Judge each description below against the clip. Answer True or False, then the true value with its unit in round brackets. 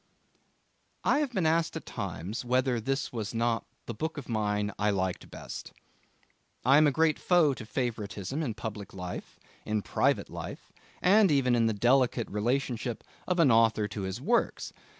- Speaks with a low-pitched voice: True (120 Hz)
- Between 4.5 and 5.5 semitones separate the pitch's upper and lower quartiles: True (5.2 semitones)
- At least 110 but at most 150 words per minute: False (170 wpm)